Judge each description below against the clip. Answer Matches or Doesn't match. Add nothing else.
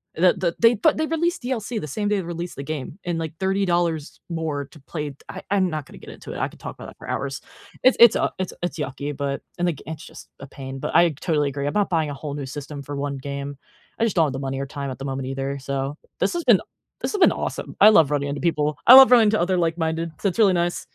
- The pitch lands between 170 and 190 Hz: Doesn't match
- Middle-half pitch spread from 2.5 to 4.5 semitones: Doesn't match